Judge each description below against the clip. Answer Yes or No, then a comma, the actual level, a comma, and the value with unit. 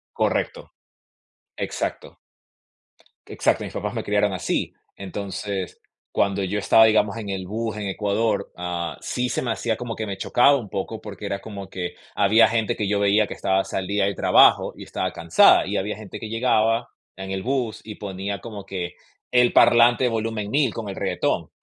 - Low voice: Yes, low, 105 Hz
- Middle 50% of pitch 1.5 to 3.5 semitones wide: Yes, narrow, 2.6 semitones